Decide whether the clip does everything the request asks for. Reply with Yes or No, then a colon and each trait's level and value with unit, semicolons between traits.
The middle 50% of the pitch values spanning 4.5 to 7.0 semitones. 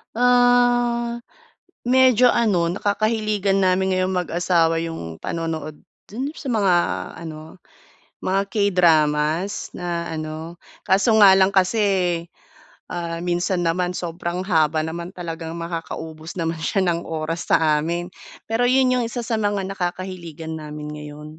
No: average, 3.9 semitones